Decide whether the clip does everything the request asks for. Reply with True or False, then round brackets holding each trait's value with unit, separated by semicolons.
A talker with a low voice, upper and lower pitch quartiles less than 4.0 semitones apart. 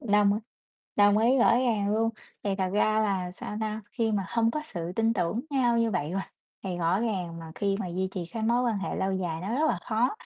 False (210 Hz; 3.4 semitones)